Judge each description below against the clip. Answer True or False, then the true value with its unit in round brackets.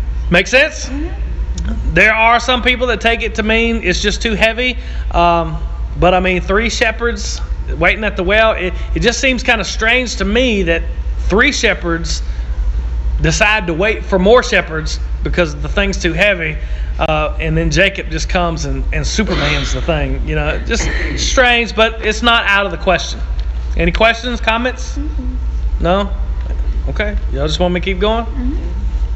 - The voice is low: False (180 Hz)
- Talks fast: False (170 wpm)